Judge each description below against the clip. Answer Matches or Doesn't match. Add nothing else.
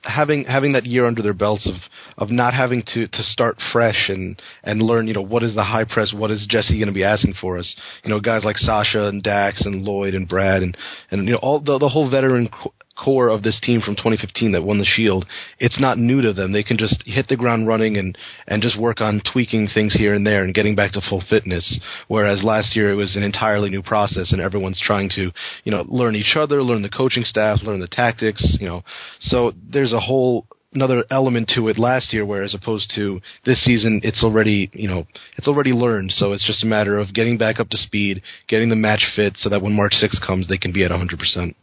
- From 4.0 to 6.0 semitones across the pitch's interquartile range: Doesn't match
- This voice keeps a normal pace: Doesn't match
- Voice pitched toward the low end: Matches